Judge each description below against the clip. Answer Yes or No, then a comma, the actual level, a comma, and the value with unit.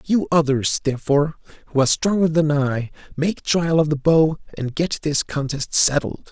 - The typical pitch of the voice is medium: Yes, medium, 150 Hz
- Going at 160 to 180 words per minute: Yes, average, 170 wpm